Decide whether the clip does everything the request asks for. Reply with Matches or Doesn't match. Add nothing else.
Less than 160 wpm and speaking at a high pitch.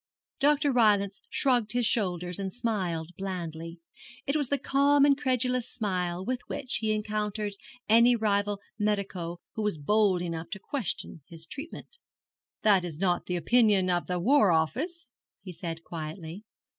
Matches